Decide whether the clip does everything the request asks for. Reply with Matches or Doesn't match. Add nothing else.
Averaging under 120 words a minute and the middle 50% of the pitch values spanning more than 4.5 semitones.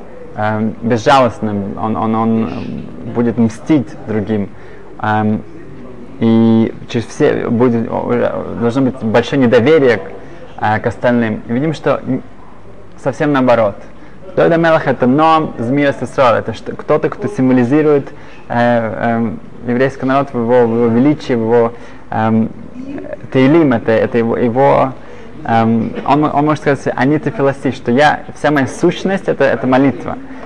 Doesn't match